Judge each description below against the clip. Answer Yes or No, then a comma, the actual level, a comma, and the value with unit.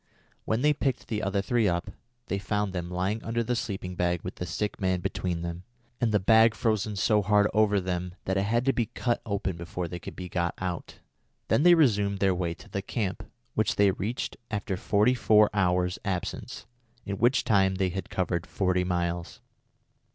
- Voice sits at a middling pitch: No, low, 100 Hz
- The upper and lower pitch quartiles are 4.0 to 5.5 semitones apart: No, average, 3.1 semitones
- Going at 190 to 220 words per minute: Yes, average, 195 wpm